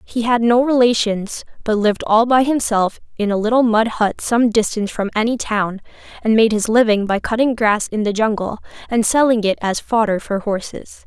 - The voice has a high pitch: Yes, high, 220 Hz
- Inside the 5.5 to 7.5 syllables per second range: No, 5.1 syllables/s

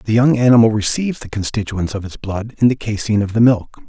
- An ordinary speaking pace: No, fast, 230 wpm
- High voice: No, low, 110 Hz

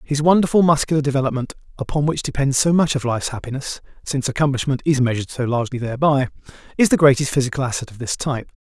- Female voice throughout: No, male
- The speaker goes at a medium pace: Yes, average, 175 wpm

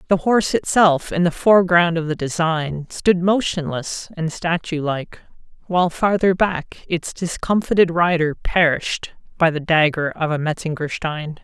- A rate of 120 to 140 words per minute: Yes, slow, 135 wpm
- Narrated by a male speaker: No, female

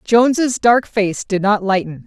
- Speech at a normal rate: Yes, average, 175 wpm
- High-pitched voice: Yes, high, 210 Hz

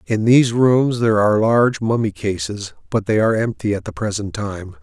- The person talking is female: No, male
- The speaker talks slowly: No, average, 200 wpm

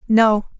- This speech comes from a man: No, female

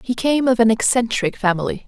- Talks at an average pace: Yes, average, 190 wpm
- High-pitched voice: Yes, high, 230 Hz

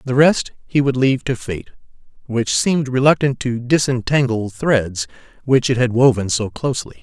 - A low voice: Yes, low, 125 Hz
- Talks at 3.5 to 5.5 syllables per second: Yes, 5.0 syllables/s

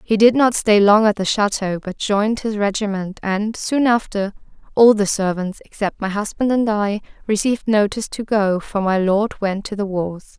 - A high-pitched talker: Yes, high, 205 Hz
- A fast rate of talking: No, average, 195 wpm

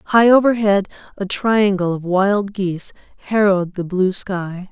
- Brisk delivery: No, average, 140 wpm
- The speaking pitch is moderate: No, high, 195 Hz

